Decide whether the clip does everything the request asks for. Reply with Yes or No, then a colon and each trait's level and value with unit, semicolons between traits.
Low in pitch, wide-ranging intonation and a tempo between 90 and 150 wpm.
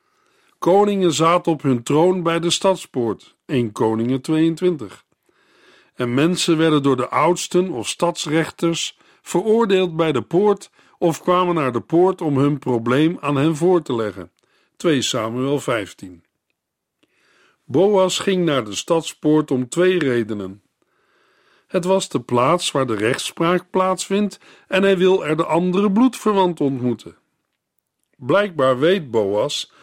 No: medium, 165 Hz; wide, 5.7 semitones; slow, 135 wpm